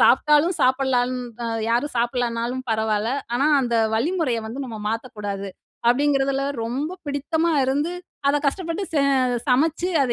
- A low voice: No, very high, 265 Hz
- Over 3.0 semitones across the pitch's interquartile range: Yes, average, 3.8 semitones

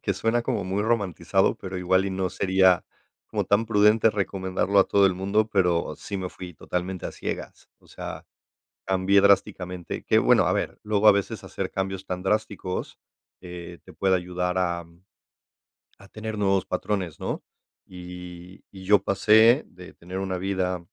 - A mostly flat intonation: Yes, narrow, 1.9 semitones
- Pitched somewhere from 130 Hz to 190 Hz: No, very low, 95 Hz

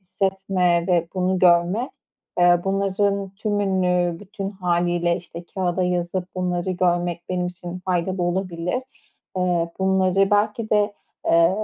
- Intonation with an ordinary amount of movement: No, narrow, 1.8 semitones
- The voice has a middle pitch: Yes, medium, 180 Hz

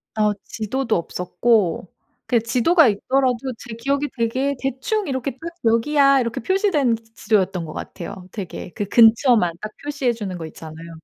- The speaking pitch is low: No, high, 230 Hz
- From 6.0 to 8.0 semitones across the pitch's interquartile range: No, wide, 5.4 semitones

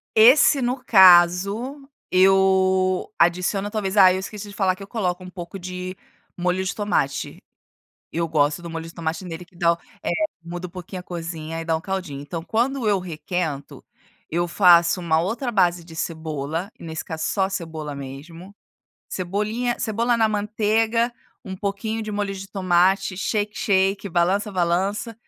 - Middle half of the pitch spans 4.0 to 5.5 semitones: No, average, 3.3 semitones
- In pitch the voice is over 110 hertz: Yes, medium, 185 Hz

